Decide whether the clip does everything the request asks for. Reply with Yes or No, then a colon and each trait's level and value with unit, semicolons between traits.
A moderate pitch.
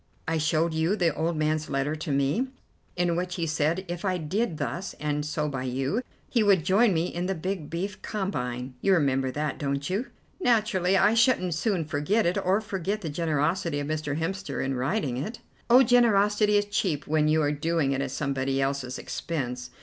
Yes: medium, 165 Hz